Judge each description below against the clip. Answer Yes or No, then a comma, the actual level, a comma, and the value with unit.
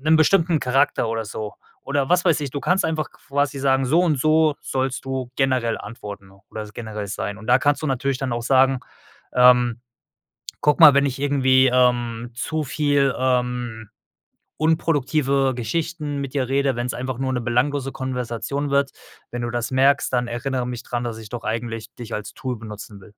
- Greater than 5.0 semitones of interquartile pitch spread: No, average, 2.9 semitones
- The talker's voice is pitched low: Yes, low, 130 Hz